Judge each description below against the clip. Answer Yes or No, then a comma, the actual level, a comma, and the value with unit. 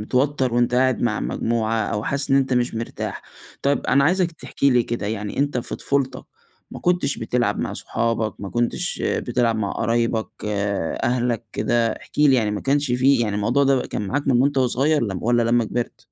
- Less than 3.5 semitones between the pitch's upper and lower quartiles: Yes, average, 3.1 semitones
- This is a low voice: Yes, low, 120 Hz